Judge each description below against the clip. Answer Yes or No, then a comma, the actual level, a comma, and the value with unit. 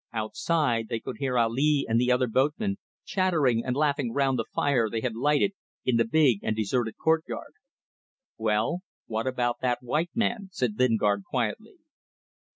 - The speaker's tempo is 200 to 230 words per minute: No, average, 160 wpm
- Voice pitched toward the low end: Yes, low, 125 Hz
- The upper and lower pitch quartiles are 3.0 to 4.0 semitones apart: No, average, 4.7 semitones